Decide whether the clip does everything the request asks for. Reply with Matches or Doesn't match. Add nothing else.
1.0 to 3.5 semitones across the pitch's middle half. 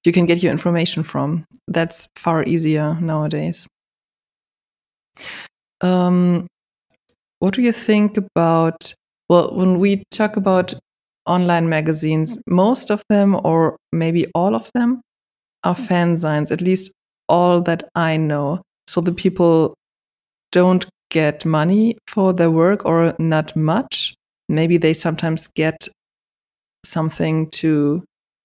Matches